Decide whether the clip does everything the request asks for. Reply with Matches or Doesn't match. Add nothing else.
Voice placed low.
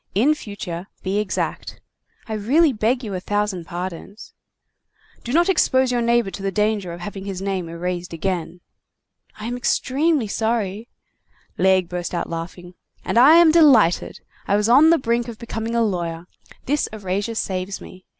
Doesn't match